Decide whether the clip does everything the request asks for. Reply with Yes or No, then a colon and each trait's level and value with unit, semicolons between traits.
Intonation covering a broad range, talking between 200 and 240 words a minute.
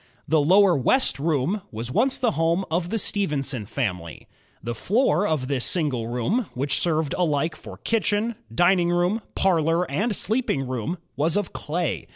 No: wide, 6.3 semitones; average, 160 wpm